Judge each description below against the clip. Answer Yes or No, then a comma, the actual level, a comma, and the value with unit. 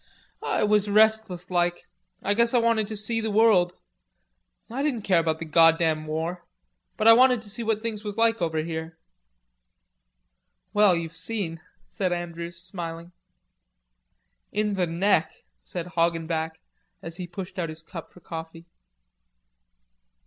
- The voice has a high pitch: No, medium, 180 Hz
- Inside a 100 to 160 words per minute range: Yes, average, 145 wpm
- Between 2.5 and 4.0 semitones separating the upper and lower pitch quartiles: No, average, 4.5 semitones